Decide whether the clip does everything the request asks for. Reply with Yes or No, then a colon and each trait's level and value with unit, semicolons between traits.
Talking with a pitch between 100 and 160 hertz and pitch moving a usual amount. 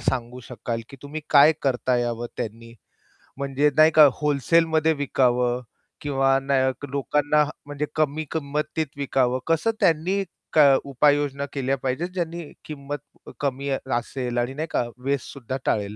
Yes: medium, 140 Hz; average, 3.0 semitones